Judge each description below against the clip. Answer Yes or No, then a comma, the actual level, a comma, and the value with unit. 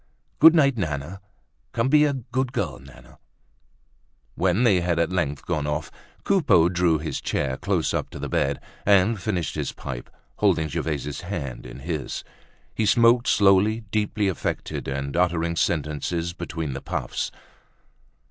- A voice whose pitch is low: Yes, very low, 85 Hz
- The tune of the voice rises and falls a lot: Yes, wide, 6.1 semitones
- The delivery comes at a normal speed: Yes, average, 150 wpm